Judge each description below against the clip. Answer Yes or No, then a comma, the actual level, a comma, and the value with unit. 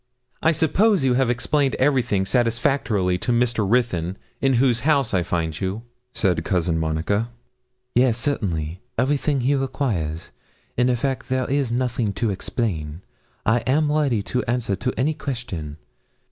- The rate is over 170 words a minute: No, average, 145 wpm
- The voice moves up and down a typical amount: No, wide, 5.8 semitones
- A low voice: Yes, low, 120 Hz